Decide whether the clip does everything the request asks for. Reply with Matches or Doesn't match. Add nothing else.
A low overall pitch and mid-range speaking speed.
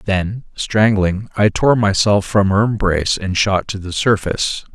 Matches